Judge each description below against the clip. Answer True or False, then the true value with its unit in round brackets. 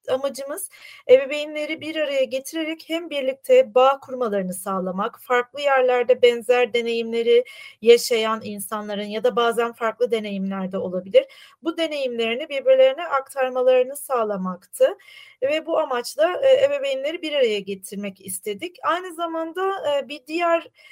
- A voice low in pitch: False (265 Hz)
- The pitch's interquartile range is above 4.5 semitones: True (4.9 semitones)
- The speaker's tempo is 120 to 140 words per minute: False (110 wpm)